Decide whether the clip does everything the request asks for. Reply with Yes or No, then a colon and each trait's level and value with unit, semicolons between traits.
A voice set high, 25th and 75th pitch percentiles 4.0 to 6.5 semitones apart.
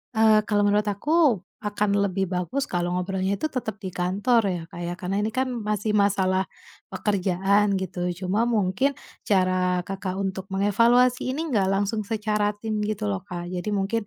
No: high, 200 Hz; narrow, 2.4 semitones